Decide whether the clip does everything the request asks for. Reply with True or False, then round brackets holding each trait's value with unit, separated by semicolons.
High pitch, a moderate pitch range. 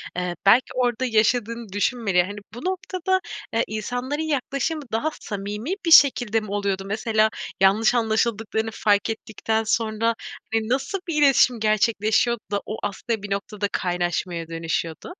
True (220 Hz; 3.3 semitones)